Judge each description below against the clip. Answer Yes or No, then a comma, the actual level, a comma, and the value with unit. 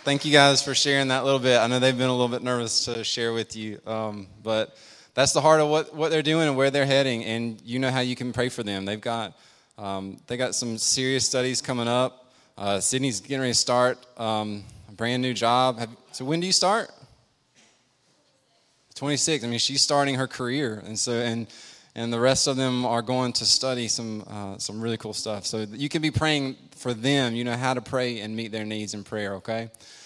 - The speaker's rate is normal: No, fast, 230 wpm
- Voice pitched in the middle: No, low, 125 Hz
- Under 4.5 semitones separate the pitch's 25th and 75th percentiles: Yes, average, 3.0 semitones